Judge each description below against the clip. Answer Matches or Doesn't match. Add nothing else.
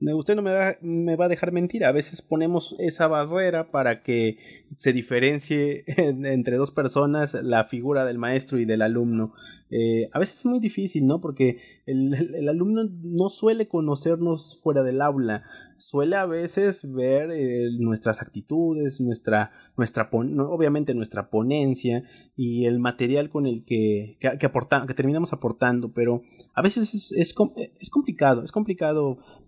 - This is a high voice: Doesn't match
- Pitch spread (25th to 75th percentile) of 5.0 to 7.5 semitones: Matches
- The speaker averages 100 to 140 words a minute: Doesn't match